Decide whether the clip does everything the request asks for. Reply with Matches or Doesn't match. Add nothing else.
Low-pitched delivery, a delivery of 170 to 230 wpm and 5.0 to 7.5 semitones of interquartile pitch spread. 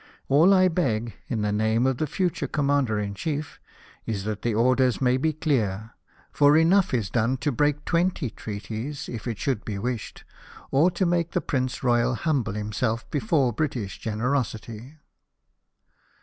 Doesn't match